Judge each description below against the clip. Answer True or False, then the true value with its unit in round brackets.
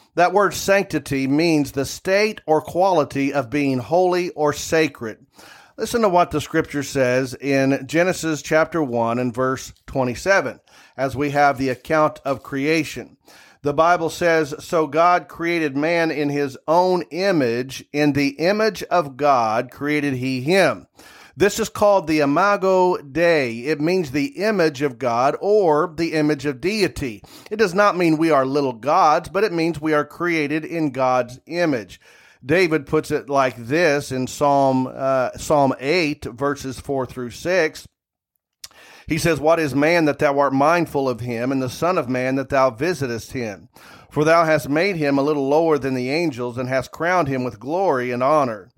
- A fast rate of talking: False (170 wpm)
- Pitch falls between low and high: True (150 Hz)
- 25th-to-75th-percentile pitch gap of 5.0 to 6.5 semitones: False (3.8 semitones)